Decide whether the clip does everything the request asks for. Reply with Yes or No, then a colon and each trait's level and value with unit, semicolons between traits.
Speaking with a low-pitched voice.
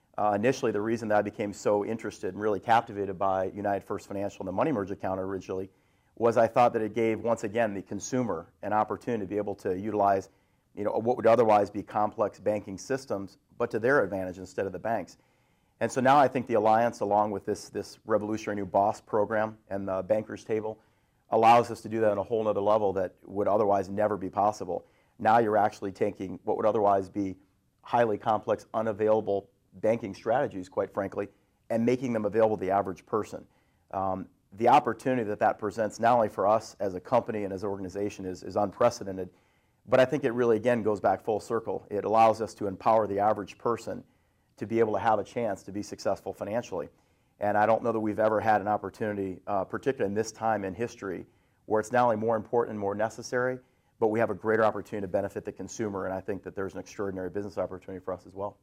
Yes: low, 105 Hz